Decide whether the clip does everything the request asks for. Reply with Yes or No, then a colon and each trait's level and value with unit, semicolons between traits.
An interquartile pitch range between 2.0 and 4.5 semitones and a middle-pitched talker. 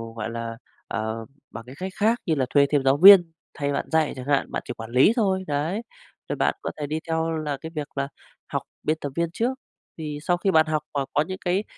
Yes: average, 4.2 semitones; medium, 155 Hz